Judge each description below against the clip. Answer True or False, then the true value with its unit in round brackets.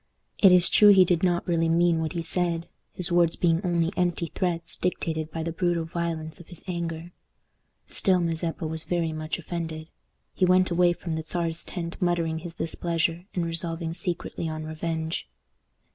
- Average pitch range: False (1.3 semitones)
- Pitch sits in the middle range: True (170 Hz)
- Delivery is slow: False (175 wpm)